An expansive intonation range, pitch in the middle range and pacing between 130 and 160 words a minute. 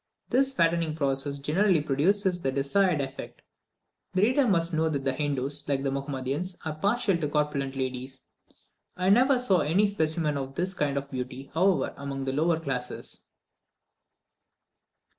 No: average, 5.0 semitones; medium, 150 Hz; average, 150 wpm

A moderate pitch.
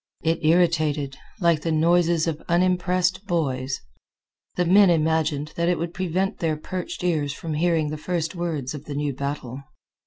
Yes: medium, 165 Hz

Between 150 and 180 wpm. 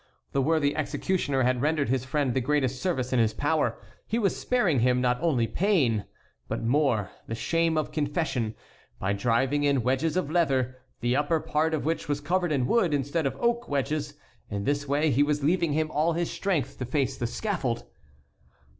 No: average, 190 wpm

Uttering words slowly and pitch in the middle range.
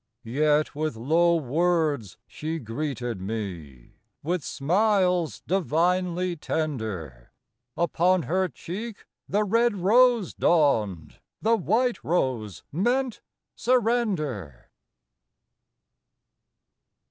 Yes: slow, 80 wpm; medium, 165 Hz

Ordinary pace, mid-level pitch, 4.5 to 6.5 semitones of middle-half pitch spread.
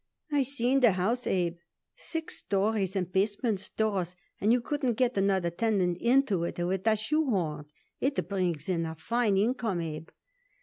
No: average, 160 wpm; high, 200 Hz; average, 5.0 semitones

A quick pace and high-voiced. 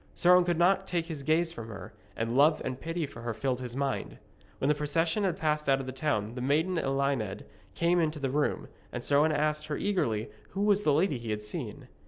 No: fast, 235 wpm; medium, 150 Hz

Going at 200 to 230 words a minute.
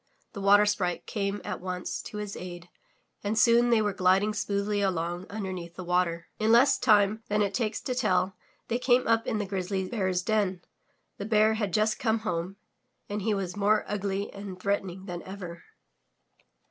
No: average, 180 wpm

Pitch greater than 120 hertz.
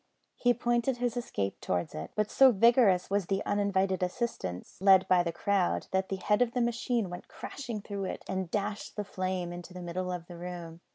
Yes: high, 190 Hz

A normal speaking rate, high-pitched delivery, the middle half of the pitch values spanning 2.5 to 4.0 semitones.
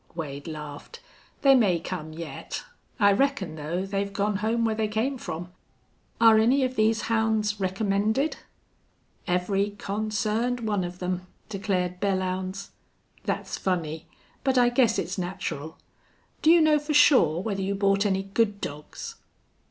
Yes: average, 145 wpm; high, 200 Hz; average, 3.7 semitones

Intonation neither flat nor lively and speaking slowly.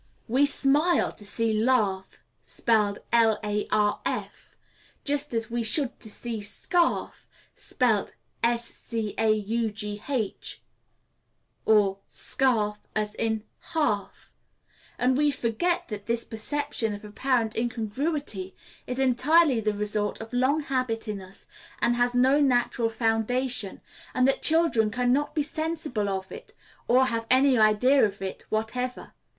Yes: average, 3.7 semitones; slow, 125 wpm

